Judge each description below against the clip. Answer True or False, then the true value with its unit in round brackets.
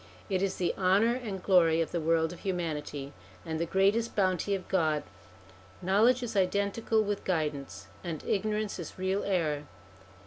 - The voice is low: False (185 Hz)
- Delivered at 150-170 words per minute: True (160 wpm)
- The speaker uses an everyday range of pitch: True (3.6 semitones)